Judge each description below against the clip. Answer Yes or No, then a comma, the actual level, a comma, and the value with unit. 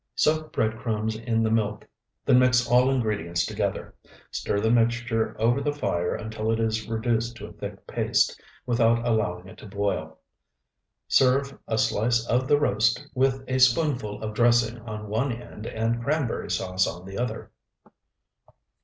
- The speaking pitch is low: Yes, low, 115 Hz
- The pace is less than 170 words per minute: Yes, average, 160 wpm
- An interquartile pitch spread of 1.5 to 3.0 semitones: Yes, narrow, 2.5 semitones